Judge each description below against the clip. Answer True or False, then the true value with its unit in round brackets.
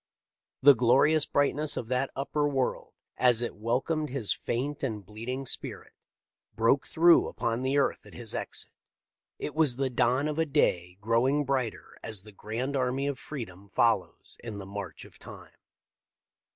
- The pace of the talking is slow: False (165 wpm)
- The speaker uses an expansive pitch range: False (4.0 semitones)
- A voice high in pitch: False (125 Hz)